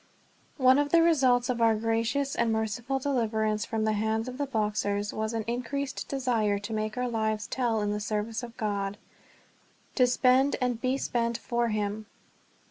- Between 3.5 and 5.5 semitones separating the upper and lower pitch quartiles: No, average, 2.8 semitones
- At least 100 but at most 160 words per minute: No, average, 175 wpm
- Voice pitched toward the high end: Yes, high, 230 Hz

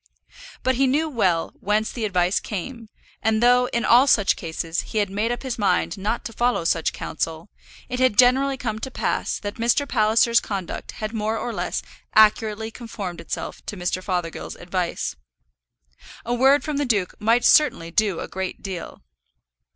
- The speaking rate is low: No, average, 175 wpm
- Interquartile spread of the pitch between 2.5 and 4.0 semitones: No, average, 4.4 semitones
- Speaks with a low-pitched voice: No, high, 220 Hz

